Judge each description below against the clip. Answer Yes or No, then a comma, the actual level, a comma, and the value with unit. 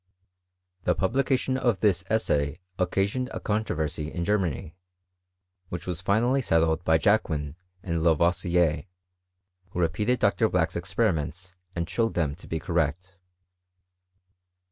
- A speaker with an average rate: No, slow, 120 wpm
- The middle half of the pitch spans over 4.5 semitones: No, average, 4.2 semitones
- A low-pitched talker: Yes, very low, 90 Hz